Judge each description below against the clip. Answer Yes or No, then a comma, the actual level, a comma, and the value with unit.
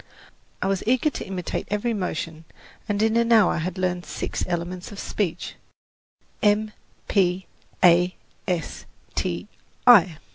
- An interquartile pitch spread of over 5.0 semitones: No, average, 3.2 semitones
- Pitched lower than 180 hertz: No, medium, 185 Hz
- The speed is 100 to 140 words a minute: Yes, slow, 135 wpm